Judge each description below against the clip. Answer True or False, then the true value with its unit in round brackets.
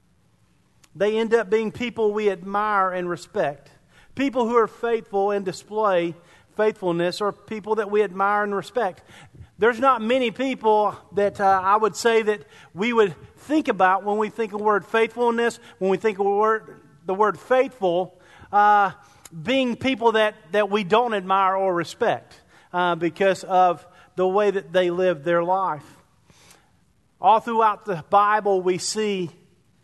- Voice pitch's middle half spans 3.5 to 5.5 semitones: False (3.0 semitones)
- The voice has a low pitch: False (205 Hz)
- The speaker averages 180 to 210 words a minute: False (155 wpm)